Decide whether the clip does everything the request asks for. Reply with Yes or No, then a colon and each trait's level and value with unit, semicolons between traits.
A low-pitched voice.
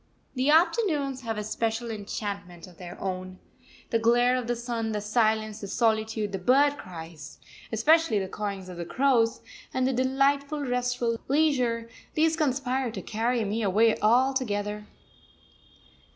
No: high, 230 Hz